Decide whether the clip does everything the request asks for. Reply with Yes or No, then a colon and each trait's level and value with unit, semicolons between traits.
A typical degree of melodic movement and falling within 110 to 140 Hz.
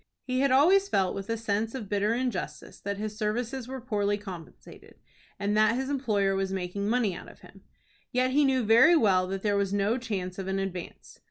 No: average, 4.4 semitones; high, 210 Hz